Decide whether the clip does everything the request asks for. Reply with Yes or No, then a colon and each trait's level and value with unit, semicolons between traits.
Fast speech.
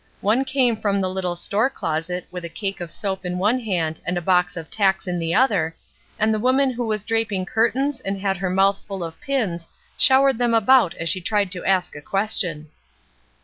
Yes: fast, 210 wpm